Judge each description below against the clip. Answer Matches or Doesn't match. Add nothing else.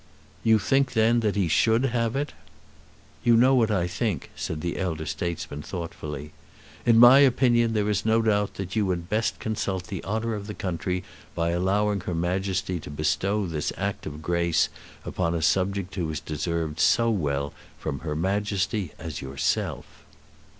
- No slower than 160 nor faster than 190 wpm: Matches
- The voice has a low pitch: Matches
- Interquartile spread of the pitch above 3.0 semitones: Matches